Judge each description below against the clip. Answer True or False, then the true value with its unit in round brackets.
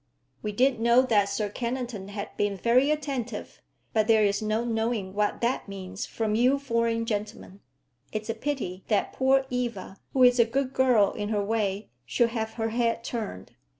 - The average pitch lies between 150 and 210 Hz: False (225 Hz)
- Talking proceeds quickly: False (180 wpm)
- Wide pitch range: False (3.1 semitones)